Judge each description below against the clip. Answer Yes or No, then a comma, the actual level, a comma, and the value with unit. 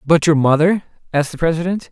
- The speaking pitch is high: No, medium, 160 Hz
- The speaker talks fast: No, average, 190 wpm